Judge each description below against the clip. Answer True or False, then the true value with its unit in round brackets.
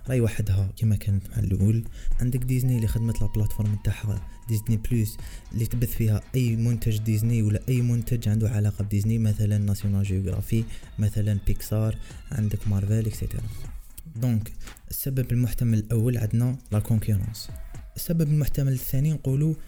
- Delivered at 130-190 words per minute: True (135 wpm)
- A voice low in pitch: True (110 Hz)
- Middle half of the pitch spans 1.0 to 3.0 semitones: True (2.5 semitones)